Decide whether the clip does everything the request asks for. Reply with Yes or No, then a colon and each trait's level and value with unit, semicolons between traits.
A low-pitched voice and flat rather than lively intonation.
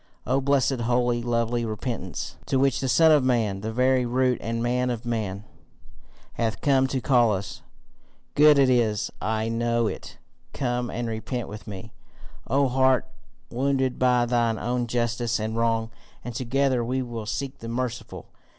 Yes: low, 120 Hz; narrow, 2.2 semitones